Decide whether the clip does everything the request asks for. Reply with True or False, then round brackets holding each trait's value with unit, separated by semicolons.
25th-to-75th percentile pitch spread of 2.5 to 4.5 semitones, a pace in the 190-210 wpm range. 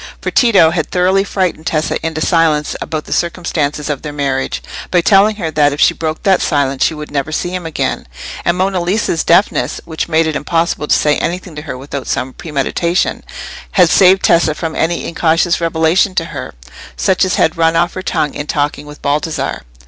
True (2.9 semitones; 195 wpm)